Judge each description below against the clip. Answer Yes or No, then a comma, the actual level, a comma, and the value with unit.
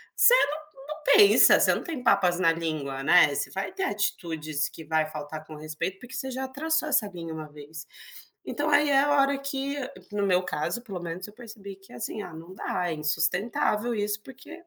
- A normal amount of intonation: No, wide, 8.8 semitones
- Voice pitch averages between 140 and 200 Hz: Yes, high, 195 Hz